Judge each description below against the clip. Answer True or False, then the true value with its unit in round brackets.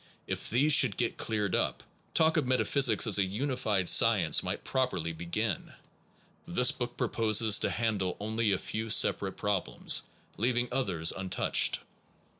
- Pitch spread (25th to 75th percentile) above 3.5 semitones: True (4.4 semitones)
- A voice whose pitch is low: True (110 Hz)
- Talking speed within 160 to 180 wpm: False (150 wpm)